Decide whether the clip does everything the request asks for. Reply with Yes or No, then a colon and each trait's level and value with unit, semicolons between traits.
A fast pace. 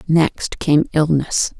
No: slow, 115 wpm